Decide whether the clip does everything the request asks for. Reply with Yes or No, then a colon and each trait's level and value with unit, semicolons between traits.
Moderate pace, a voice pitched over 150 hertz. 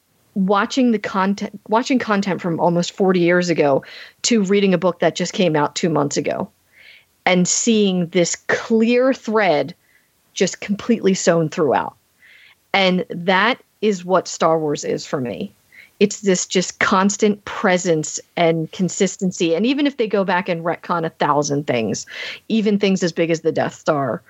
Yes: average, 160 wpm; medium, 185 Hz